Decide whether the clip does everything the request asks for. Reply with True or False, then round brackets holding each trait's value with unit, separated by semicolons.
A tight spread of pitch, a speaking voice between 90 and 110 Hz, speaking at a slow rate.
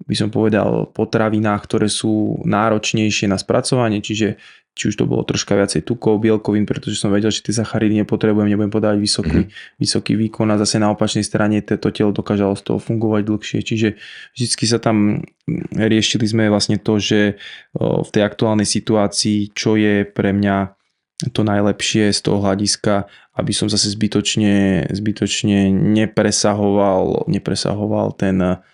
False (1.2 semitones; 105 Hz; 150 wpm)